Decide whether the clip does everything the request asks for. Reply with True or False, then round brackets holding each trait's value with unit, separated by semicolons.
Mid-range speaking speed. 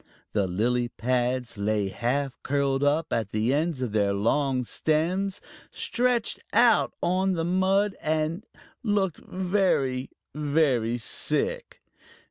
False (115 wpm)